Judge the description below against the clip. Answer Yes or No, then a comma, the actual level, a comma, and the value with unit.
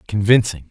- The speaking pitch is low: Yes, low, 105 Hz